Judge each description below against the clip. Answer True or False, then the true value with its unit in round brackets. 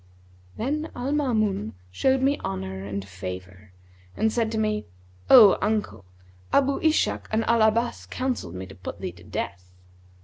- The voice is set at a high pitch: True (215 Hz)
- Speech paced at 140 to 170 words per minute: True (150 wpm)